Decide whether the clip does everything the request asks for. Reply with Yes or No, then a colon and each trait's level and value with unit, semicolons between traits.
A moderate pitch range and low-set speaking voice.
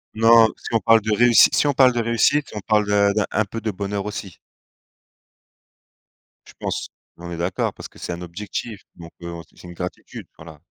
Yes: average, 4.4 semitones; low, 105 Hz